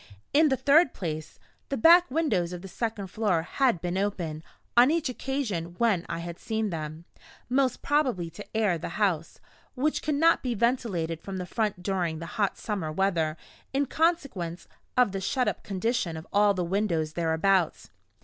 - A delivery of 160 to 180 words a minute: Yes, average, 175 wpm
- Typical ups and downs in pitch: No, wide, 6.7 semitones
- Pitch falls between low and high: No, high, 200 Hz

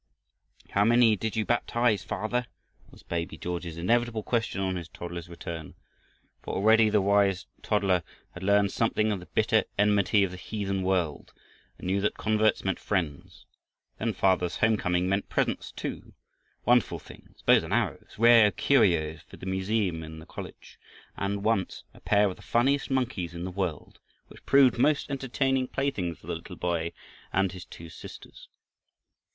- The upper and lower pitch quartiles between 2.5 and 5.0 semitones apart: Yes, average, 3.9 semitones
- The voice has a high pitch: No, low, 100 Hz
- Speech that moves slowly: No, average, 165 wpm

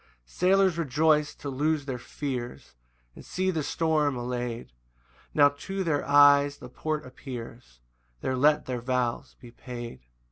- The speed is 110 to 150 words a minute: Yes, average, 145 wpm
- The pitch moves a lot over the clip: No, average, 3.6 semitones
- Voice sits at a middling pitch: Yes, medium, 145 Hz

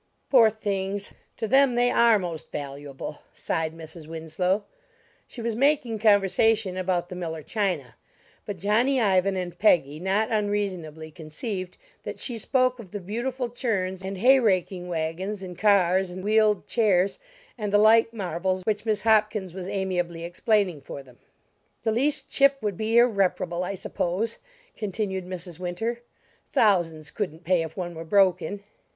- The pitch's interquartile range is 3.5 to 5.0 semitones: Yes, average, 3.8 semitones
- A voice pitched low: No, high, 195 Hz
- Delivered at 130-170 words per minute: Yes, average, 150 wpm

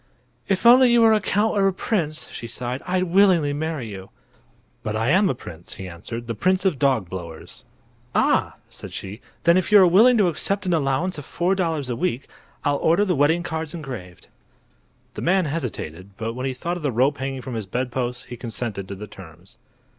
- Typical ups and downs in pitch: No, wide, 7.8 semitones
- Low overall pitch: No, medium, 145 Hz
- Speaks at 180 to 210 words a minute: Yes, fast, 205 wpm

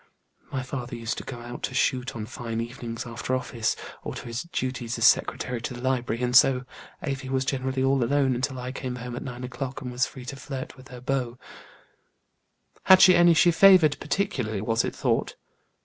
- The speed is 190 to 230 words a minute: Yes, average, 200 wpm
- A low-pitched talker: Yes, low, 125 Hz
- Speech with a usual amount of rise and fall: No, narrow, 1.8 semitones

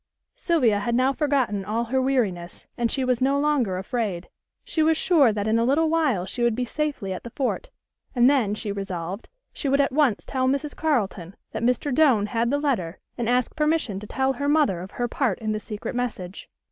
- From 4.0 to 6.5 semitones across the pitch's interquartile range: Yes, average, 5.3 semitones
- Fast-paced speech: Yes, fast, 210 wpm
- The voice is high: Yes, high, 245 Hz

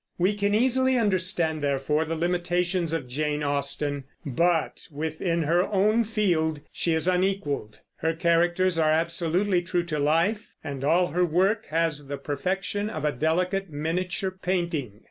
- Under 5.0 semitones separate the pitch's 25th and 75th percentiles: Yes, average, 3.4 semitones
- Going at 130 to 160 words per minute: Yes, average, 145 wpm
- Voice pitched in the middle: Yes, medium, 170 Hz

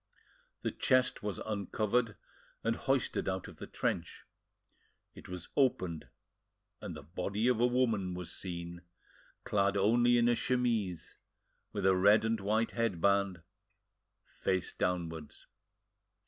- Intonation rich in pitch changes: No, average, 4.2 semitones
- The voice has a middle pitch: No, low, 100 Hz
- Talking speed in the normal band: No, slow, 125 wpm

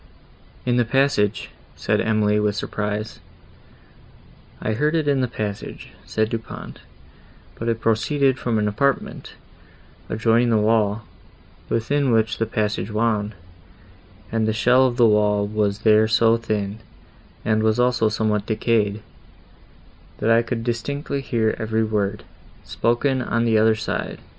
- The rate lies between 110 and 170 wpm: Yes, average, 140 wpm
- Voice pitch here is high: No, low, 110 Hz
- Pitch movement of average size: No, narrow, 1.8 semitones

